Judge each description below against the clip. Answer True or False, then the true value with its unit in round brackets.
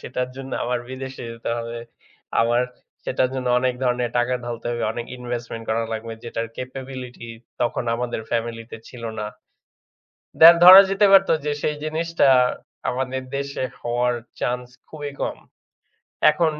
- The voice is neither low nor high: False (125 Hz)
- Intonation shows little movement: True (2.2 semitones)